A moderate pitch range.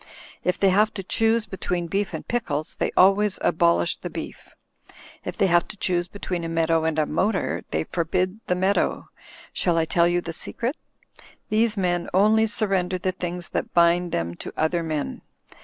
Yes: average, 3.1 semitones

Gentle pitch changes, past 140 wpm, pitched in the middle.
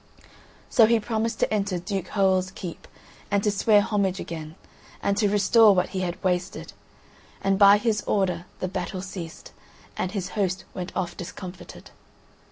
No: narrow, 2.2 semitones; average, 160 wpm; high, 195 Hz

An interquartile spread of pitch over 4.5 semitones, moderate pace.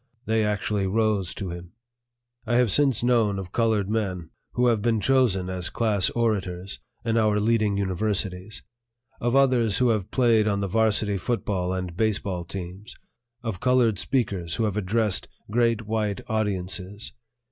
No: average, 3.3 semitones; average, 150 wpm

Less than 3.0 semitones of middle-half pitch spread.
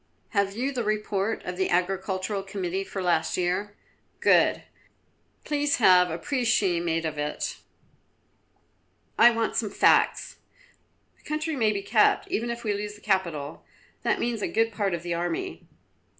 No: average, 4.0 semitones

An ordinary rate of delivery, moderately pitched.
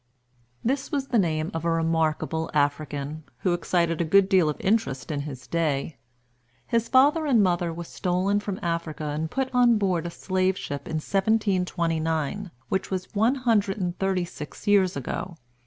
Yes: average, 170 wpm; medium, 175 Hz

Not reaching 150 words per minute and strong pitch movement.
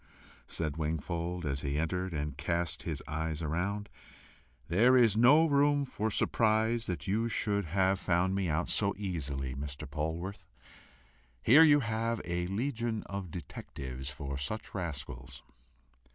Yes: slow, 135 wpm; wide, 6.4 semitones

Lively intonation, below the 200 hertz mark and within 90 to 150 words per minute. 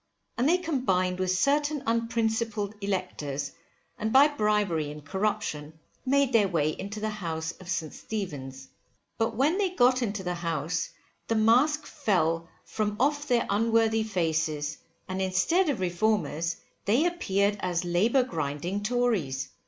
No: wide, 5.8 semitones; high, 205 Hz; average, 140 wpm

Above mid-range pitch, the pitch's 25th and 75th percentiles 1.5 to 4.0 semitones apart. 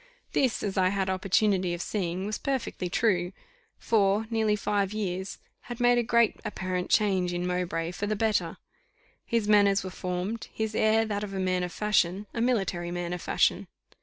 Yes: high, 195 Hz; average, 3.1 semitones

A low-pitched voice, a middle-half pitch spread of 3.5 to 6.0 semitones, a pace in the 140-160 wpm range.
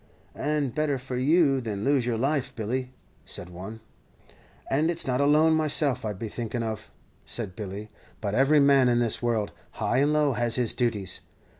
No: low, 125 Hz; average, 4.1 semitones; average, 175 wpm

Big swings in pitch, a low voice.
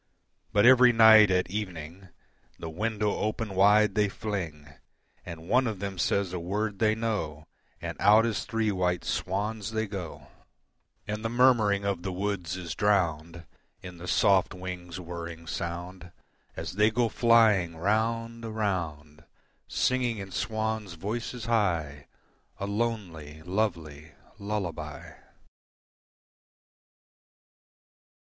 No: average, 4.2 semitones; low, 100 Hz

